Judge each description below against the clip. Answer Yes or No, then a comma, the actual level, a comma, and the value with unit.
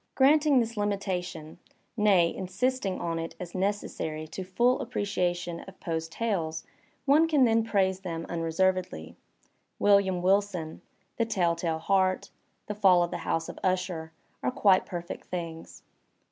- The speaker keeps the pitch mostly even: No, average, 3.5 semitones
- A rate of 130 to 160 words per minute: Yes, average, 150 wpm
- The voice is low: No, medium, 185 Hz